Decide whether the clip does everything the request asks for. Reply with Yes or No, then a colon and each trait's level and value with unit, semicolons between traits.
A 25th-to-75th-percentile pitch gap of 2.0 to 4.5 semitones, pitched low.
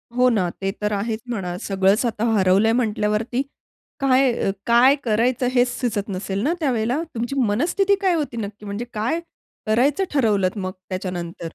No: average, 4.0 semitones; high, 225 Hz